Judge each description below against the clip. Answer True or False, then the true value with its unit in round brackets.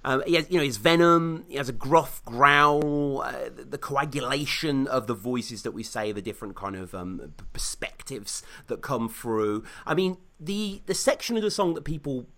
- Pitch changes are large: True (6.4 semitones)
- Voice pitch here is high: False (140 Hz)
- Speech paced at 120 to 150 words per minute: False (195 wpm)